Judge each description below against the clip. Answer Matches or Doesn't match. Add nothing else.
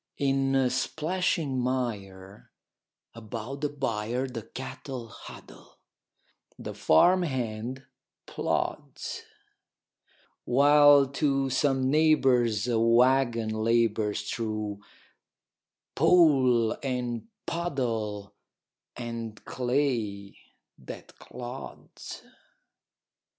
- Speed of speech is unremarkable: Doesn't match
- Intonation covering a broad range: Doesn't match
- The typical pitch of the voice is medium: Doesn't match